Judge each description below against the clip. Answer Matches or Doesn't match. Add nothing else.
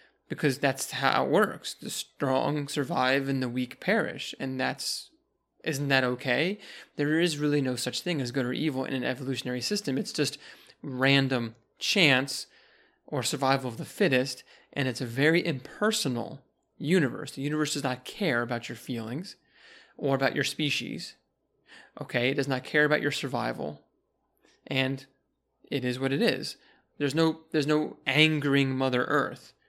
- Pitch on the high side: Doesn't match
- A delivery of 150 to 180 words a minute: Matches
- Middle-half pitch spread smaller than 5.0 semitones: Matches